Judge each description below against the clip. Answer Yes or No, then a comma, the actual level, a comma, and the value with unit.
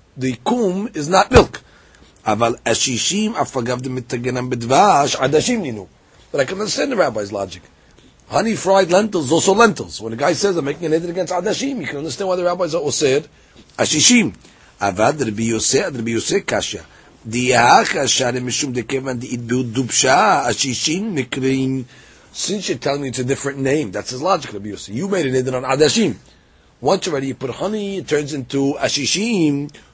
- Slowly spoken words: Yes, slow, 125 wpm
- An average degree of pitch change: No, wide, 6.4 semitones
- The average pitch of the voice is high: No, low, 135 Hz